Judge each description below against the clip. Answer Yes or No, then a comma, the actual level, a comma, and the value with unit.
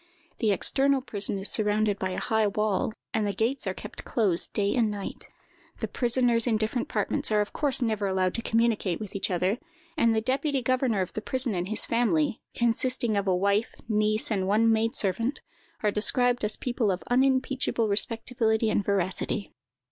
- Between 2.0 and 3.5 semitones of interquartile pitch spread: Yes, average, 3.1 semitones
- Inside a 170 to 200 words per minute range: Yes, average, 185 wpm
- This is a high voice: Yes, high, 220 Hz